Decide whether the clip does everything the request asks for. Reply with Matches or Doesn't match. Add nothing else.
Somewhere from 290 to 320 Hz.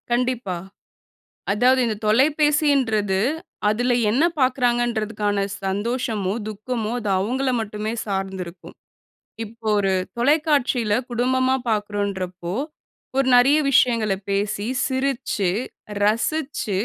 Doesn't match